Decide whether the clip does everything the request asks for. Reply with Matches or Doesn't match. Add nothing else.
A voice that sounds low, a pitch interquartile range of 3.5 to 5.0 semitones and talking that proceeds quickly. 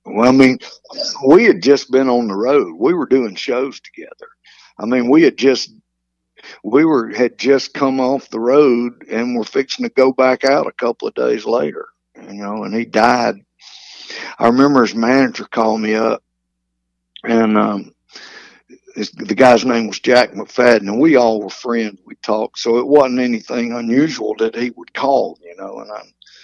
Doesn't match